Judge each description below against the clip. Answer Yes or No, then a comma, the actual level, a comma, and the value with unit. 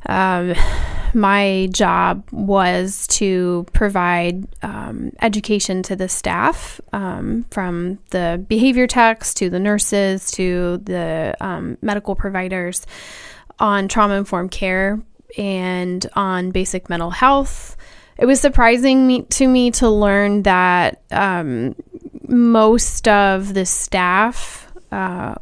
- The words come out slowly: Yes, slow, 115 wpm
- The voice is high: Yes, high, 195 Hz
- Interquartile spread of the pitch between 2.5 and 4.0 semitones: Yes, average, 3.4 semitones